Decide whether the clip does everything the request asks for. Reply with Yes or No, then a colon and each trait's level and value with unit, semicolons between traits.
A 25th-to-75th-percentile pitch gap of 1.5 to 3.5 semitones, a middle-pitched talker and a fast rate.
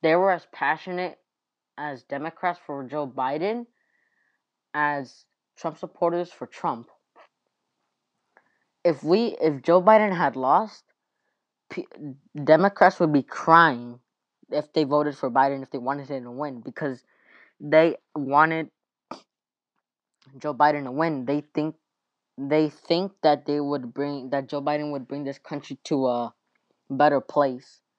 No: average, 3.1 semitones; medium, 150 Hz; slow, 135 wpm